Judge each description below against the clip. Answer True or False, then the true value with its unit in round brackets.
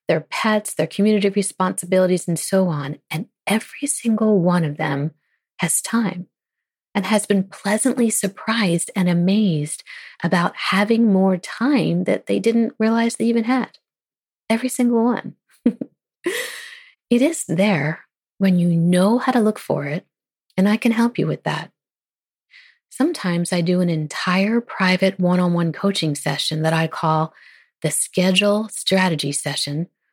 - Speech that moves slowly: False (145 wpm)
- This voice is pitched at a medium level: False (195 Hz)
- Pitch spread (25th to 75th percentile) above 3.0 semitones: True (5.0 semitones)